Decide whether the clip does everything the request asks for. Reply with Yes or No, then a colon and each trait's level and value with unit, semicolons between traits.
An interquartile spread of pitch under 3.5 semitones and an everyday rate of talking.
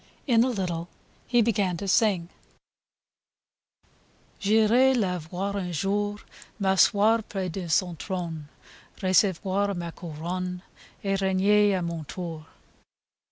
No: average, 2.9 semitones; slow, 115 wpm